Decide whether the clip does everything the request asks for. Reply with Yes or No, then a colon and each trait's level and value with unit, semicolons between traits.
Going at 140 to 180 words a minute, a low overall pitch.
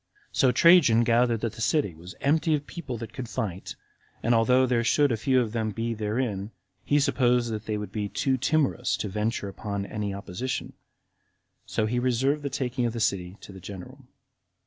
No: average, 190 wpm; low, 115 Hz